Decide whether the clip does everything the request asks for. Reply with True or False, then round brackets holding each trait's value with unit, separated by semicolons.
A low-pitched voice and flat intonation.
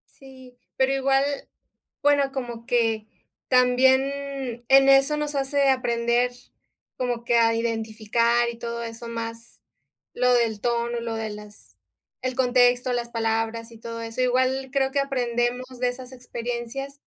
False (245 Hz; 2.3 semitones)